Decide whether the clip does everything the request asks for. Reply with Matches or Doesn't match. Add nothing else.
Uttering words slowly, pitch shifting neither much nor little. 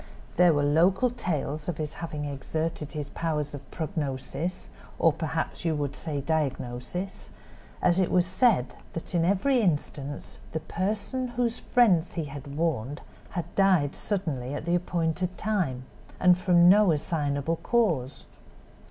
Doesn't match